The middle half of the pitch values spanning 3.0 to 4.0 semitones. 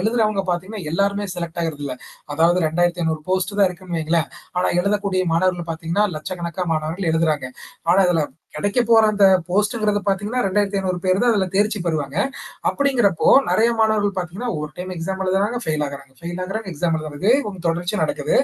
Yes: average, 3.7 semitones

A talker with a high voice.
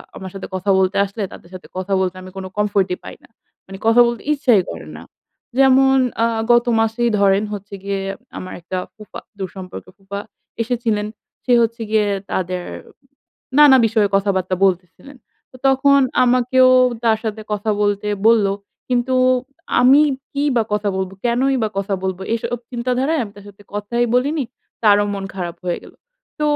Yes: high, 210 Hz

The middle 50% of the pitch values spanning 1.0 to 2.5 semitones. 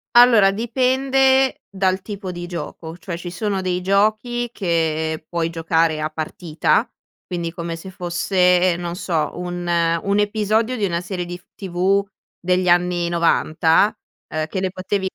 No: average, 2.9 semitones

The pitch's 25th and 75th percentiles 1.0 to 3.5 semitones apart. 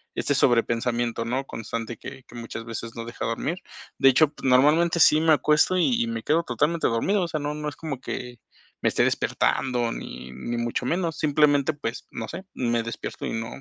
No: average, 5.0 semitones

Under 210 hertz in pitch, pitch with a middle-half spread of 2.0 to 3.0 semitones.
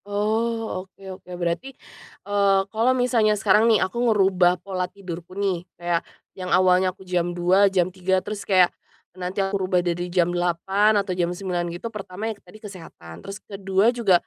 Yes: high, 190 Hz; narrow, 2.4 semitones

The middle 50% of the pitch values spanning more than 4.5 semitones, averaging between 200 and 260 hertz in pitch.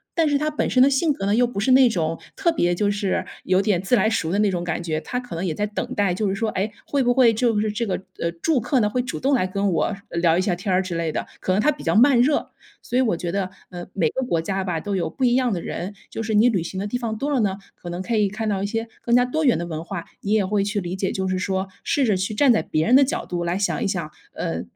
Yes: average, 5.1 semitones; high, 205 Hz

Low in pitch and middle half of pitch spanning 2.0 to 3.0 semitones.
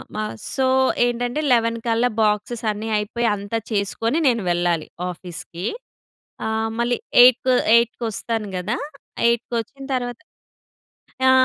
No: high, 230 Hz; average, 2.7 semitones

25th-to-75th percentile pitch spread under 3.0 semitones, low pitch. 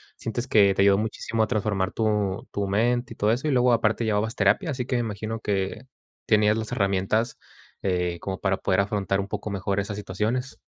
Yes: narrow, 2.5 semitones; low, 105 Hz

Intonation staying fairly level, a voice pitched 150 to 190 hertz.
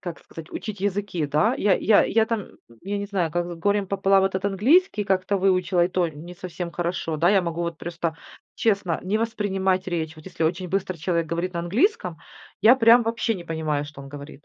No: average, 3.3 semitones; medium, 185 Hz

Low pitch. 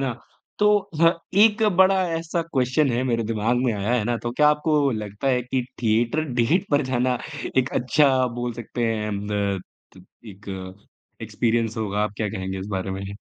Yes: low, 120 Hz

